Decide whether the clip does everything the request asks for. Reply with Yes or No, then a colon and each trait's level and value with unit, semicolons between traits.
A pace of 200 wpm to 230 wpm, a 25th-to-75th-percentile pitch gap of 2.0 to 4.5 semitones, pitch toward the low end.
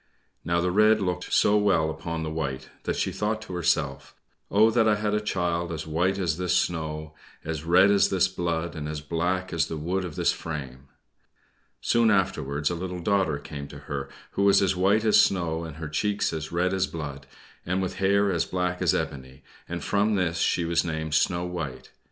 Yes: fast, 205 wpm; average, 3.4 semitones; very low, 85 Hz